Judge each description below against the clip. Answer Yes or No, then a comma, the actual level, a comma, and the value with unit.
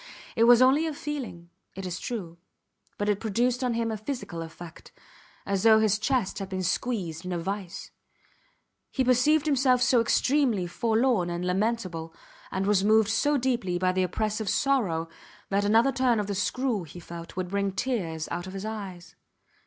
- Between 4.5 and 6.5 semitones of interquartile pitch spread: Yes, average, 5.1 semitones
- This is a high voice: Yes, high, 210 Hz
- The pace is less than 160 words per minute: No, average, 175 wpm